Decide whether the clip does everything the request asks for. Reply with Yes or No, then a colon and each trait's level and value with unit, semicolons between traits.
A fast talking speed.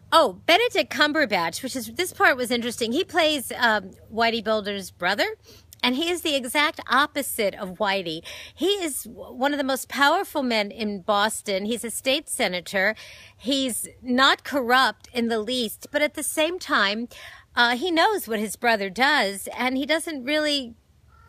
No: average, 165 wpm